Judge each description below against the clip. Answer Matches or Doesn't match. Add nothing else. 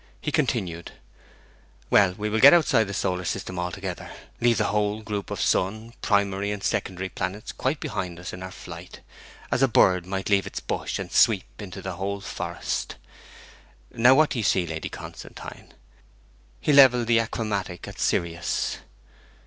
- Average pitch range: Matches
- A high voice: Doesn't match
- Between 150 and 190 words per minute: Matches